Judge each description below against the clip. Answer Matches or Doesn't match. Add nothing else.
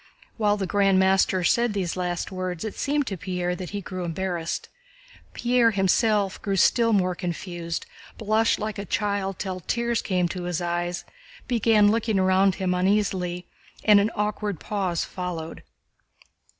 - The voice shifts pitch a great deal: Doesn't match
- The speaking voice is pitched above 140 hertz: Matches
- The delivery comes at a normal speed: Matches